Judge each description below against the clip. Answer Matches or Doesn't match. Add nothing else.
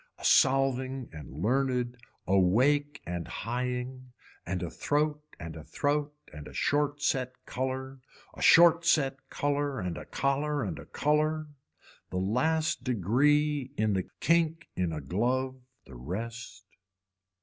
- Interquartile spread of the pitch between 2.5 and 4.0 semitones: Doesn't match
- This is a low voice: Matches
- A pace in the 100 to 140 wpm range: Matches